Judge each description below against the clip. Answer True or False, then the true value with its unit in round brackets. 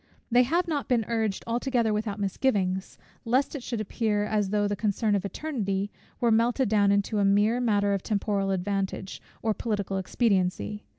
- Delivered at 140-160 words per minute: False (170 wpm)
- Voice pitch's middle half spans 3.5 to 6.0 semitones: False (2.8 semitones)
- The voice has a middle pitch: False (210 Hz)